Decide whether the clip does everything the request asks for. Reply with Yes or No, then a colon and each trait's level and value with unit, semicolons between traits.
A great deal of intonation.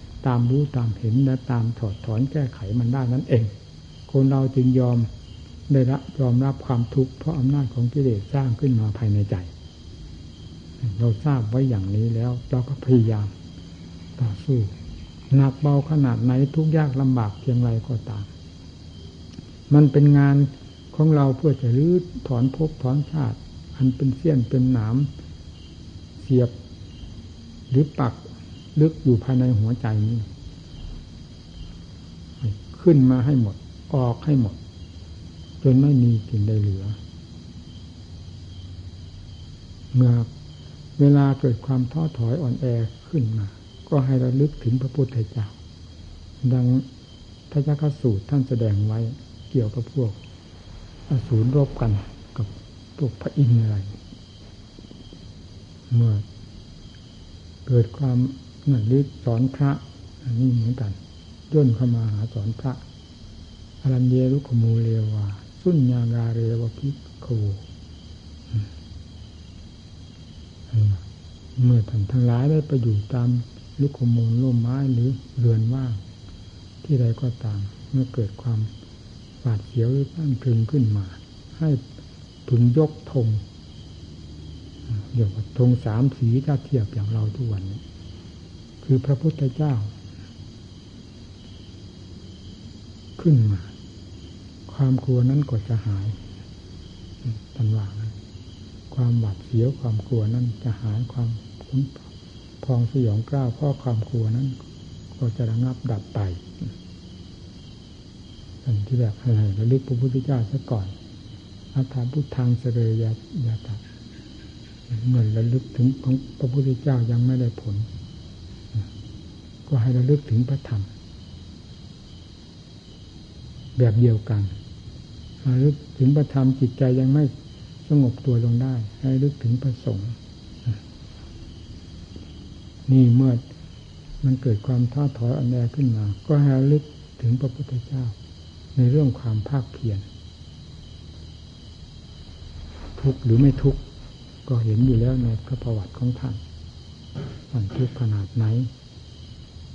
No: average, 4.7 semitones